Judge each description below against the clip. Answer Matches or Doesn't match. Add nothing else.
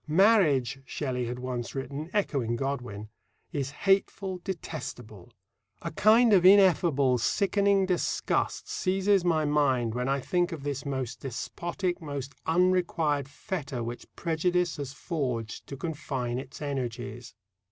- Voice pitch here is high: Doesn't match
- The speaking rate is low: Matches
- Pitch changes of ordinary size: Doesn't match